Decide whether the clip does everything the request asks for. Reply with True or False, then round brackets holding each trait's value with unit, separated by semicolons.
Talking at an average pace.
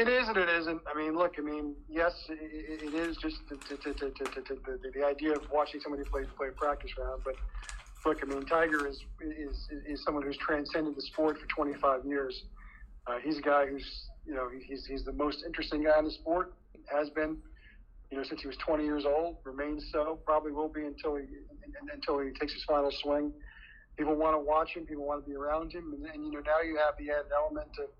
False (230 wpm)